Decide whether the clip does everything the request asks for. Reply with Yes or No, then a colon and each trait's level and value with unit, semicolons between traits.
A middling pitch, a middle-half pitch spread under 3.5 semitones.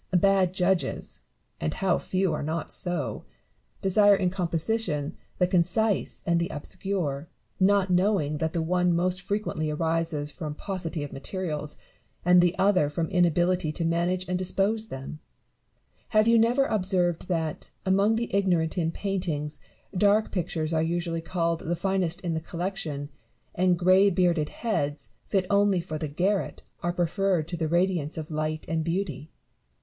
Yes: medium, 175 Hz; average, 3.1 semitones